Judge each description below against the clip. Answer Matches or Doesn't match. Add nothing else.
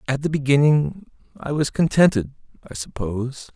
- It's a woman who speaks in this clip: Doesn't match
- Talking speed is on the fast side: Doesn't match